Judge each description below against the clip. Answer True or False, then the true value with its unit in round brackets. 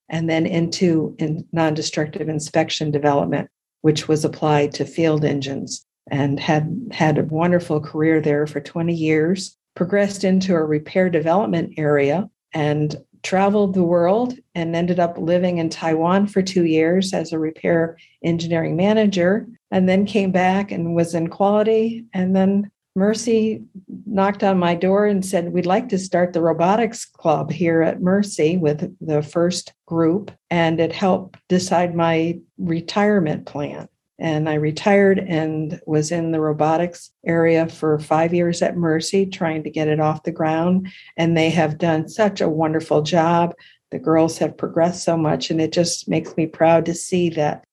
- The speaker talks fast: False (160 wpm)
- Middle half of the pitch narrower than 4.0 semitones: True (2.9 semitones)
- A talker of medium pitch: True (170 Hz)